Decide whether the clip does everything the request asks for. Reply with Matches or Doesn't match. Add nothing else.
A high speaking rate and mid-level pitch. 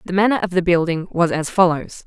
Matches